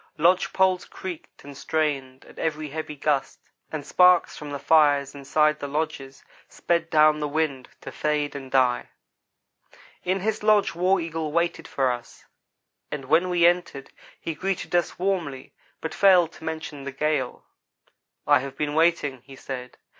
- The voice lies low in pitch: No, medium, 150 Hz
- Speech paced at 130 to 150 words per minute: No, average, 160 wpm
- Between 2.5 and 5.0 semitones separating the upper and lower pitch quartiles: Yes, average, 3.5 semitones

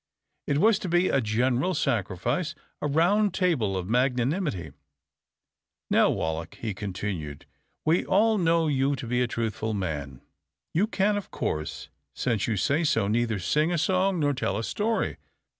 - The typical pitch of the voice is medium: No, low, 130 Hz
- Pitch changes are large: Yes, wide, 8.6 semitones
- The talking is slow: No, average, 160 wpm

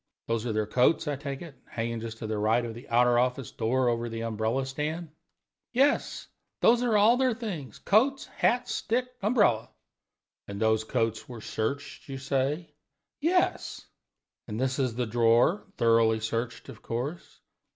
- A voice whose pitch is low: Yes, low, 125 Hz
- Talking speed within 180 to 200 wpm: No, average, 165 wpm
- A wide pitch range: Yes, wide, 6.4 semitones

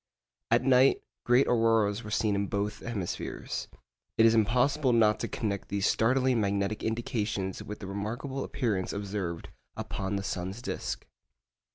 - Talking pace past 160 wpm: No, average, 145 wpm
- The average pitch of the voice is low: Yes, low, 105 Hz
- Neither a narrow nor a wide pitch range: Yes, average, 3.1 semitones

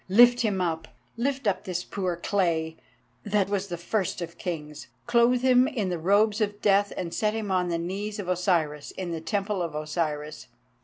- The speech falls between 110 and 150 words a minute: No, average, 190 wpm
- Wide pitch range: No, average, 3.8 semitones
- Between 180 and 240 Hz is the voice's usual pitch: Yes, high, 190 Hz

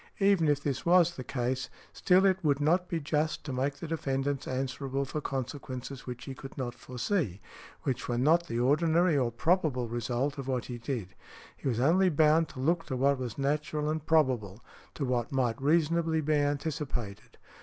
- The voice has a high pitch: No, medium, 140 Hz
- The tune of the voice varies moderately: Yes, average, 3.8 semitones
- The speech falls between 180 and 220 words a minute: Yes, average, 185 wpm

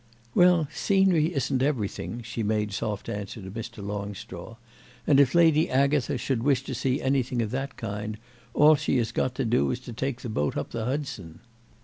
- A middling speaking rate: Yes, average, 190 wpm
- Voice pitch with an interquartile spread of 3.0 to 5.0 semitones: Yes, average, 4.6 semitones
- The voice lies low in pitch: Yes, low, 125 Hz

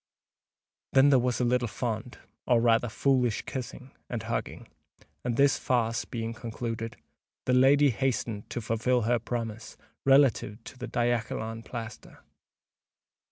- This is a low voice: Yes, low, 120 Hz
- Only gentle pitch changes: Yes, narrow, 2.0 semitones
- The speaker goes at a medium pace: No, slow, 125 wpm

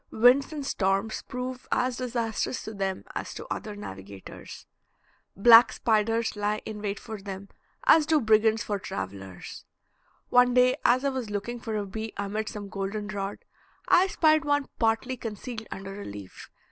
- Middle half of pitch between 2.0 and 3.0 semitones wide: No, average, 3.8 semitones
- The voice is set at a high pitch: Yes, high, 220 Hz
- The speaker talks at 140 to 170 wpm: Yes, average, 160 wpm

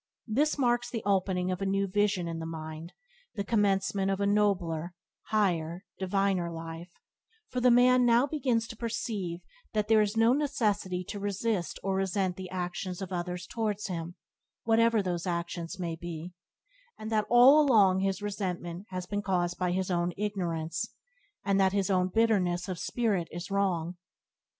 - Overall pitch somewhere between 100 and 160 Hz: No, high, 195 Hz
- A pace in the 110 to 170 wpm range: Yes, average, 165 wpm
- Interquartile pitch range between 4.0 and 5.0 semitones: No, average, 3.3 semitones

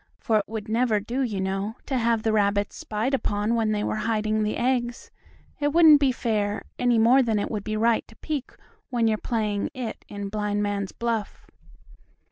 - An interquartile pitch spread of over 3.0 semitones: No, narrow, 2.5 semitones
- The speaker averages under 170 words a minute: No, average, 195 wpm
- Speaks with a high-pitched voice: Yes, high, 220 Hz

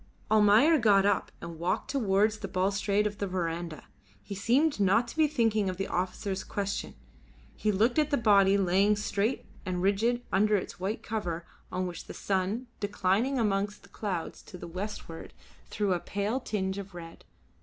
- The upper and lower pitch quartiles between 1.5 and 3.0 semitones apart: Yes, narrow, 2.6 semitones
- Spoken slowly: No, average, 175 wpm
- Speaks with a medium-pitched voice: No, high, 200 Hz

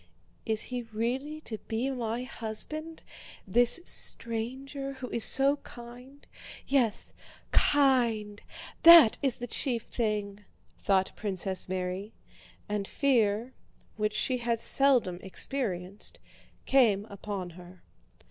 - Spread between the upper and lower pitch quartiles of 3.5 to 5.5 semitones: Yes, average, 4.4 semitones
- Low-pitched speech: No, high, 230 Hz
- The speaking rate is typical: No, slow, 105 wpm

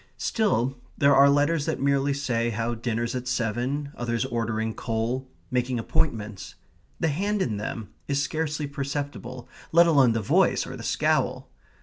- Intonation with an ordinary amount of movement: Yes, average, 3.5 semitones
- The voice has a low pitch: Yes, low, 130 Hz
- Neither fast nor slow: Yes, average, 150 wpm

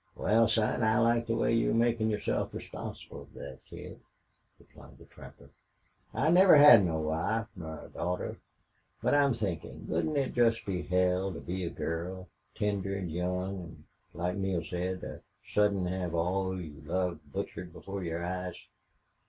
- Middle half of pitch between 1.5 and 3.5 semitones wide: No, average, 4.0 semitones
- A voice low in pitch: Yes, very low, 95 Hz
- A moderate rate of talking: Yes, average, 160 wpm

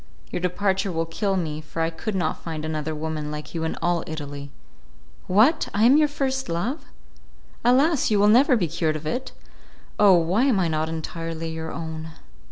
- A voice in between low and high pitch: Yes, medium, 170 Hz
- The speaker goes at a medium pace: Yes, average, 185 wpm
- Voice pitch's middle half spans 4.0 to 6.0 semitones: Yes, average, 5.2 semitones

